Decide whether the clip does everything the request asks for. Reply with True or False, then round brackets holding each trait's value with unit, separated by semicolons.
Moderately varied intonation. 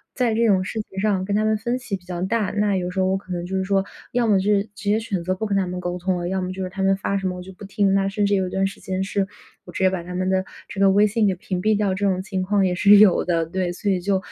False (1.8 semitones)